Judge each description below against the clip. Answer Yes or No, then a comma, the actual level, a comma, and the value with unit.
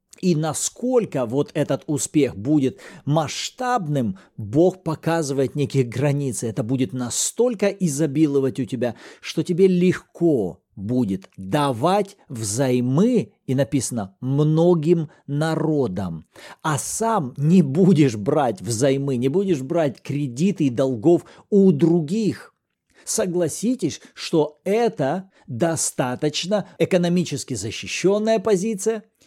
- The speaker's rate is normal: No, slow, 100 wpm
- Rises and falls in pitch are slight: No, average, 5.3 semitones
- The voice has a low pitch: No, medium, 155 Hz